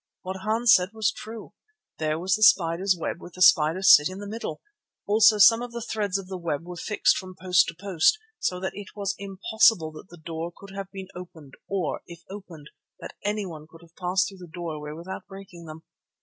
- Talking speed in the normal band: No, fast, 210 wpm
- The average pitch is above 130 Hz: Yes, medium, 185 Hz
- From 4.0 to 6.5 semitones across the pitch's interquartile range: No, average, 3.3 semitones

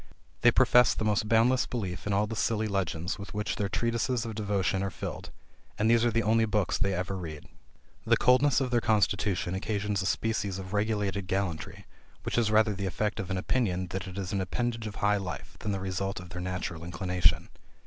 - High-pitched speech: No, low, 100 Hz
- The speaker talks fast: Yes, fast, 210 wpm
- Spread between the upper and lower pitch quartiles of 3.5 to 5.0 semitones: No, average, 2.9 semitones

